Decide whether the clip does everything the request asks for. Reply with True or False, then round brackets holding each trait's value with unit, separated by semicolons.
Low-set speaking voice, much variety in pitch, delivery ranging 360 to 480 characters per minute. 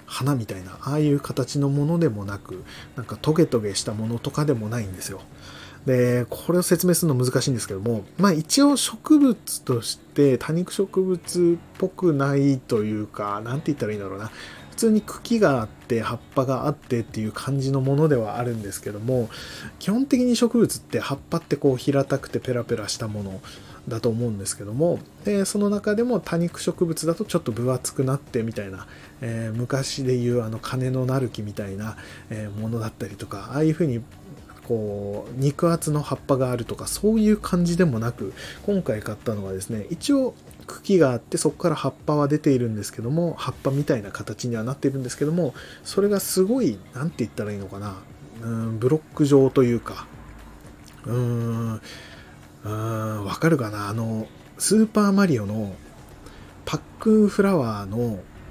True (130 Hz; 6.8 semitones; 370 characters per minute)